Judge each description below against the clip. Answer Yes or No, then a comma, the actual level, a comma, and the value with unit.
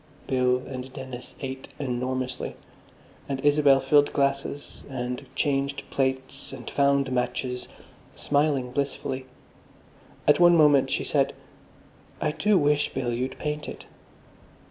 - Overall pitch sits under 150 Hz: Yes, low, 135 Hz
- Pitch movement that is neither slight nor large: No, narrow, 2.0 semitones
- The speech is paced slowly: Yes, slow, 120 wpm